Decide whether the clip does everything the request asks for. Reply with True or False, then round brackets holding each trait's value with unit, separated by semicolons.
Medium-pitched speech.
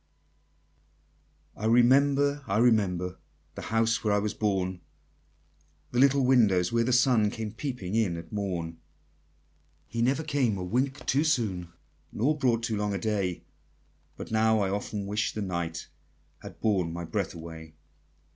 False (110 Hz)